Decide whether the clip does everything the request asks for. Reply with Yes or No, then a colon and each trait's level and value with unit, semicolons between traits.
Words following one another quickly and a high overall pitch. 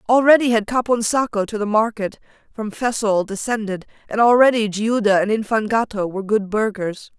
No: average, 140 wpm; high, 215 Hz